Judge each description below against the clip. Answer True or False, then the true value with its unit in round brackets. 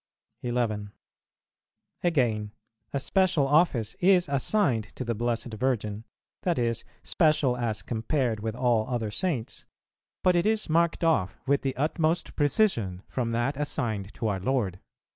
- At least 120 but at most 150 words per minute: True (140 wpm)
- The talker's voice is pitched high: False (125 Hz)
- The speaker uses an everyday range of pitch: False (5.9 semitones)